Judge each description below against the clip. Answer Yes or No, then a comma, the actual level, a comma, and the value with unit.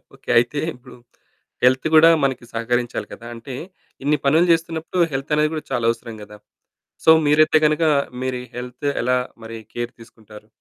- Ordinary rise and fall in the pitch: Yes, average, 4.2 semitones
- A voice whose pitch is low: Yes, low, 125 Hz